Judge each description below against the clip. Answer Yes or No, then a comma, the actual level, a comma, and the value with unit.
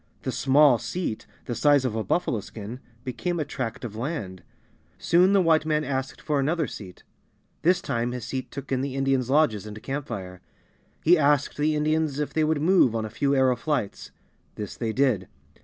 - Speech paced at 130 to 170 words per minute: No, average, 190 wpm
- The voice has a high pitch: No, low, 135 Hz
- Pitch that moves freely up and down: No, average, 4.8 semitones